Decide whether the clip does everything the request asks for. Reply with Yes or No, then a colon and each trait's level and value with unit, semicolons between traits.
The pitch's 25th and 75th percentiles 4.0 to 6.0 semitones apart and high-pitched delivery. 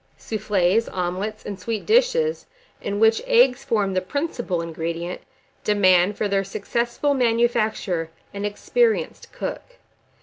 Yes: average, 4.4 semitones; high, 210 Hz